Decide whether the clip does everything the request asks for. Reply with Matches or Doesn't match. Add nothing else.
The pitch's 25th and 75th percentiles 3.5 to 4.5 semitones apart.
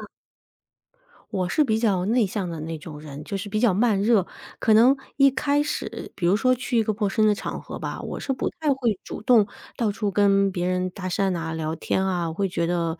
Matches